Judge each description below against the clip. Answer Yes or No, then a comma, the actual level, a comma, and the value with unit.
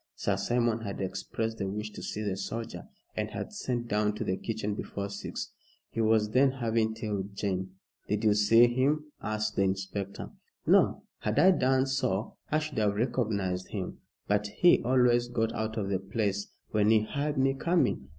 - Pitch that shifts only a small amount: No, average, 3.1 semitones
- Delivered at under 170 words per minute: No, average, 185 wpm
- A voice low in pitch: Yes, low, 110 Hz